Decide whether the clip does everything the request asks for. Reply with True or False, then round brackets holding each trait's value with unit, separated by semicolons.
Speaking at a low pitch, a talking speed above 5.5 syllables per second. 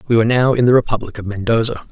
True (115 Hz; 7.5 syllables/s)